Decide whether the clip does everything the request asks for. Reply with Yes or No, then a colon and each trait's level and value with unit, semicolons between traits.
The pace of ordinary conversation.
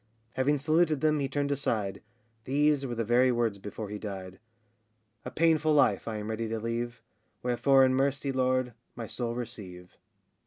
Yes: average, 165 wpm